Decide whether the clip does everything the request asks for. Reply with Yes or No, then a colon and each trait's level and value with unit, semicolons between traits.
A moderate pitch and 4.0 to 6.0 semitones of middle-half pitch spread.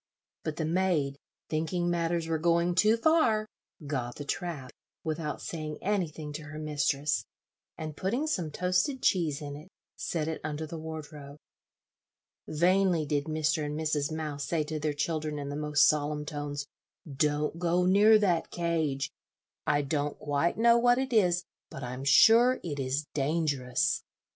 No: medium, 155 Hz; average, 3.0 semitones